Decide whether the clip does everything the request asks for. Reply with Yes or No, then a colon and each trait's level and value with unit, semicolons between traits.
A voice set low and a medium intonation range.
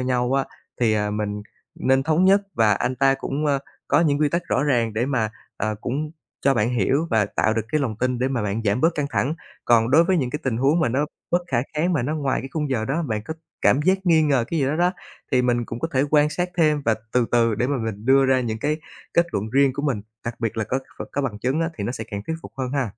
Yes: low, 130 Hz; average, 4.5 semitones